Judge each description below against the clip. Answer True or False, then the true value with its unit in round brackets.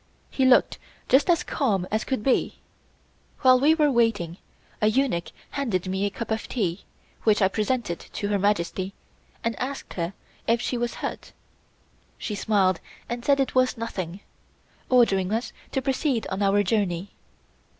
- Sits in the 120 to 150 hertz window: False (220 Hz)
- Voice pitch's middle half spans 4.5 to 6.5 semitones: True (4.9 semitones)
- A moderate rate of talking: True (160 wpm)